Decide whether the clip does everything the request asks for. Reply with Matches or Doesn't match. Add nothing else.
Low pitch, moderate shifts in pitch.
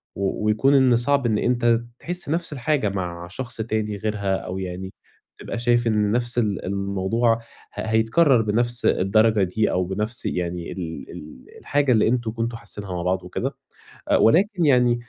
Matches